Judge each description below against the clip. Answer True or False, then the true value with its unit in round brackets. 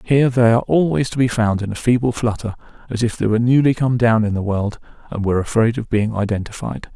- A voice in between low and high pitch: False (115 Hz)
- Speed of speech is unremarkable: False (235 wpm)